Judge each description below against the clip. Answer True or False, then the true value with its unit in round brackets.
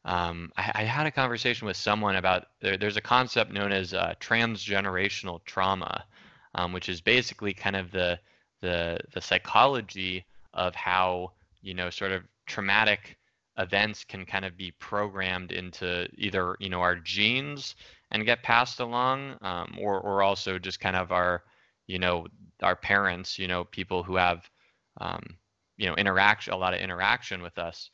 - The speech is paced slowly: False (170 wpm)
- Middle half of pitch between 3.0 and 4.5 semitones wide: False (2.6 semitones)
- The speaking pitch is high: False (95 Hz)